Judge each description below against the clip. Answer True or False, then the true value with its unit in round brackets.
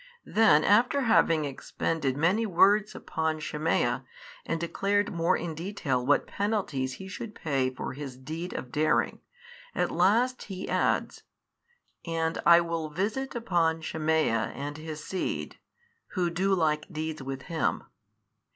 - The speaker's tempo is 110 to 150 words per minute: True (140 wpm)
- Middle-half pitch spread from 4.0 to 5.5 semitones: True (4.3 semitones)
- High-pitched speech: False (165 Hz)